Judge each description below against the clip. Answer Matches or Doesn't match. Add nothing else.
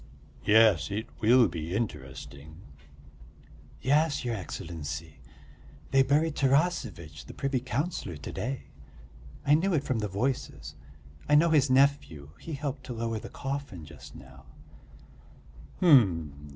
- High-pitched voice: Doesn't match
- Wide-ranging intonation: Matches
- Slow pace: Matches